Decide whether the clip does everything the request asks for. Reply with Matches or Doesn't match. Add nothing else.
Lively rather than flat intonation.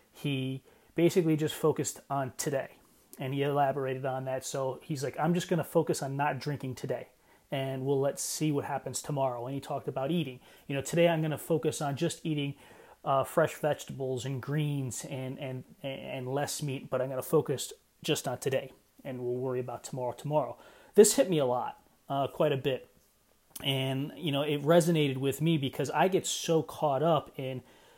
Doesn't match